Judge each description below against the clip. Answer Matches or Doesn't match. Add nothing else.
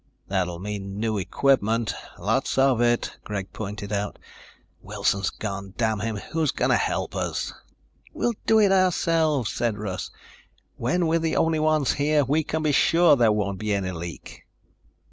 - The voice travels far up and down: Matches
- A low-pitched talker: Matches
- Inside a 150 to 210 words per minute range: Matches